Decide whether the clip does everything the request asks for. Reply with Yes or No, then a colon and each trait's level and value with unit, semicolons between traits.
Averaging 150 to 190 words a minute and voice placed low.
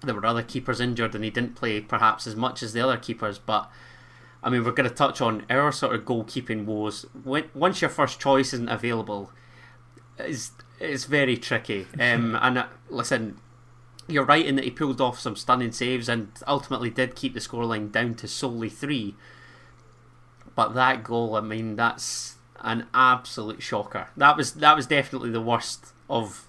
Yes: average, 185 wpm; low, 120 Hz